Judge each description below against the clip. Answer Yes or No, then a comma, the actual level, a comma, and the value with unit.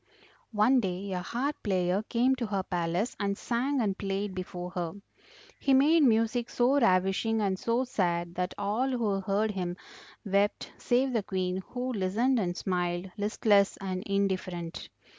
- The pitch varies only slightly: No, average, 4.3 semitones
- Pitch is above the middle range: Yes, high, 200 Hz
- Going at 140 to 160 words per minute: Yes, average, 155 wpm